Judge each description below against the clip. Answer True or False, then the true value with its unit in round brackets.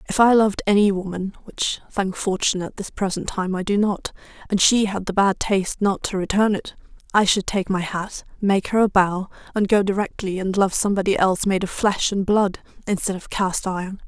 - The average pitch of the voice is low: False (195 Hz)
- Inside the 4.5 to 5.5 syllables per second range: True (5.4 syllables/s)